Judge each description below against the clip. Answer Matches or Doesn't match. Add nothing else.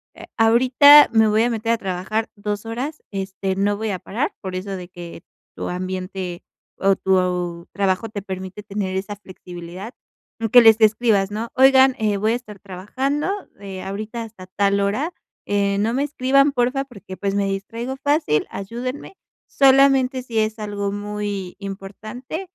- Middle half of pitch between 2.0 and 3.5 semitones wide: Doesn't match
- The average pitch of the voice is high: Matches